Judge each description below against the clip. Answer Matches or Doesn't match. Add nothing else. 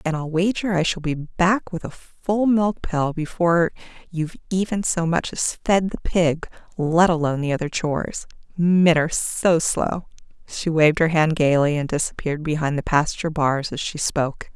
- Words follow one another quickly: Doesn't match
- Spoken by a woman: Matches